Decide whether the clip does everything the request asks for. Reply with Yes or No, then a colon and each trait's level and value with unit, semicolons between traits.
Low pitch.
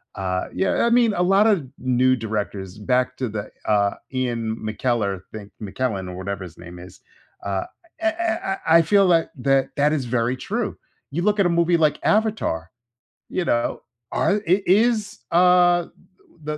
Yes: low, 130 Hz